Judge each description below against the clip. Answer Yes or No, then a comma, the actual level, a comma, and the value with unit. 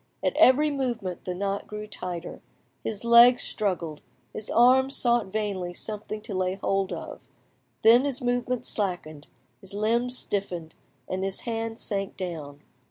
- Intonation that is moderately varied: Yes, average, 4.3 semitones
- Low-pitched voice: No, high, 210 Hz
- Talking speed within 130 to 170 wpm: Yes, average, 145 wpm